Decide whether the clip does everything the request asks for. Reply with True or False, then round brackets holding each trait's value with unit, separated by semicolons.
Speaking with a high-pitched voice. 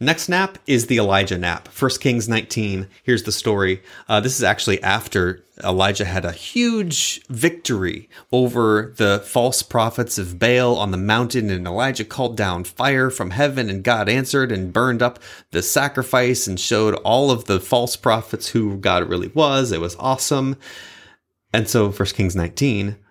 False (110 Hz)